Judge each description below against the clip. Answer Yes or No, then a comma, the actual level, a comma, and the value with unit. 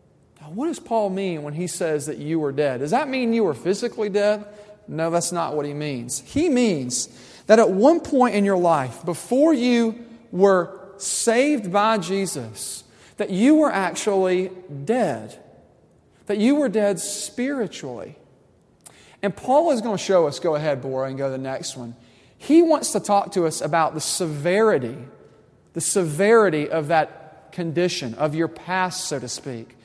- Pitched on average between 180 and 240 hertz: Yes, medium, 185 Hz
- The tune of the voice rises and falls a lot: Yes, wide, 6.2 semitones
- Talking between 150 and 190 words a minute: Yes, average, 170 wpm